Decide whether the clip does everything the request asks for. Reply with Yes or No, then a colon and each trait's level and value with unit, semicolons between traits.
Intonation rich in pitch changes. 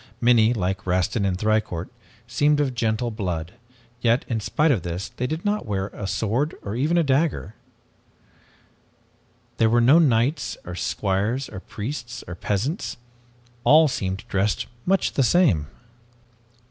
Yes: wide, 6.0 semitones